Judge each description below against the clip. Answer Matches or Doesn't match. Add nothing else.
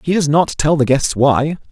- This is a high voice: Doesn't match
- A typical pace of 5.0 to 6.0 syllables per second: Doesn't match